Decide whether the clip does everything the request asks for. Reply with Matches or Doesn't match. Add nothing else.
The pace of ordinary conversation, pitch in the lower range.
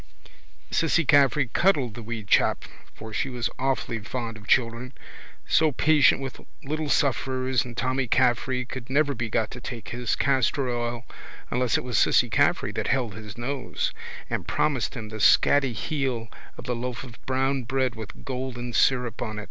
Matches